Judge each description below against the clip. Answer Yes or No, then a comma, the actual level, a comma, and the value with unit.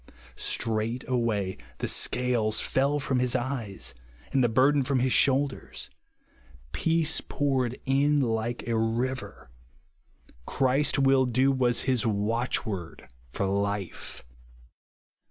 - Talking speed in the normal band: No, slow, 110 wpm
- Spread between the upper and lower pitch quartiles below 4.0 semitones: Yes, average, 3.2 semitones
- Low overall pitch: Yes, low, 125 Hz